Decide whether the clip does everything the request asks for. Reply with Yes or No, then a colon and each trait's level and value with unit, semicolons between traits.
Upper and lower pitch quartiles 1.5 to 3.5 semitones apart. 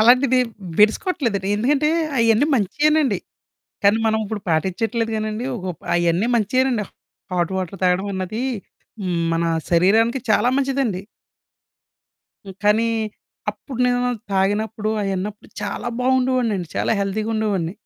No: average, 4.2 semitones